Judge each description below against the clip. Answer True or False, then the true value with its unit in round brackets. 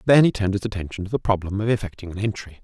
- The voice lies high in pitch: False (100 Hz)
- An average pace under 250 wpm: False (275 wpm)